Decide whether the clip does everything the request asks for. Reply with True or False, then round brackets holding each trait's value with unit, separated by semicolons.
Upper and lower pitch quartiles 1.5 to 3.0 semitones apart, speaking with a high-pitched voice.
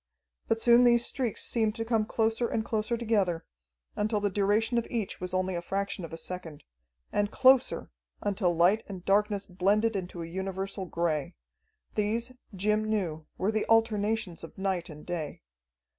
False (3.6 semitones; 205 Hz)